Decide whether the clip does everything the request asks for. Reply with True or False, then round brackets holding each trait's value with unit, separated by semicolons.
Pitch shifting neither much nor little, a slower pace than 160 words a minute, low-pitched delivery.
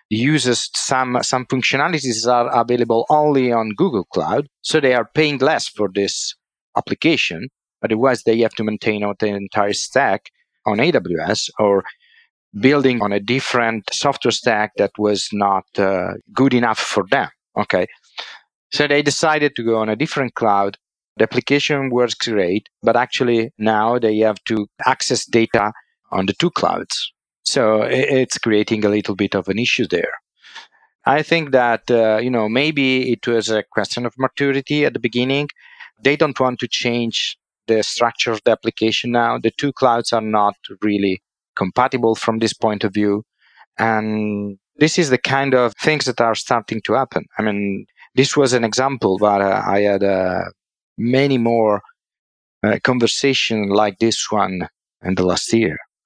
False (3.6 semitones; 165 wpm; 115 Hz)